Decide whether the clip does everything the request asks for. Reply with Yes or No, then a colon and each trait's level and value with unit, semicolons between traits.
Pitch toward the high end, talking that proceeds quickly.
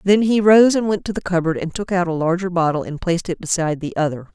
No: medium, 180 Hz; fast, 275 wpm